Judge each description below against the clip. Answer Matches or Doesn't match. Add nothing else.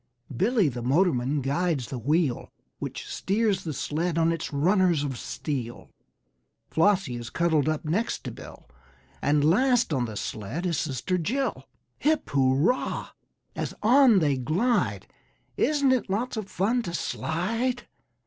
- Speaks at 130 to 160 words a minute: Matches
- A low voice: Doesn't match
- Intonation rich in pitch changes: Matches